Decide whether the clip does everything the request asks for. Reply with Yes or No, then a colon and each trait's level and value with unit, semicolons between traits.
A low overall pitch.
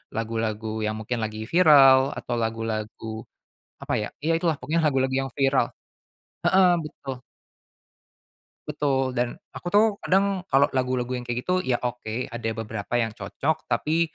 Yes: low, 130 Hz